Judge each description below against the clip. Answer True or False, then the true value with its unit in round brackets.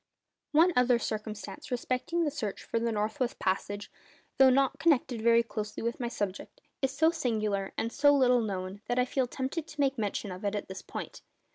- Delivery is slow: False (195 wpm)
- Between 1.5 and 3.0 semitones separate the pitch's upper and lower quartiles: False (4.3 semitones)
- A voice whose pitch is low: False (235 Hz)